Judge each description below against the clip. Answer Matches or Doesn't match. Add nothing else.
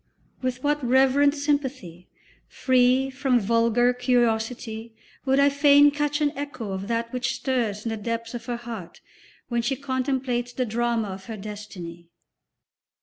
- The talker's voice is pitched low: Doesn't match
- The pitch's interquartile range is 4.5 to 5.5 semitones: Doesn't match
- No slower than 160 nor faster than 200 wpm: Doesn't match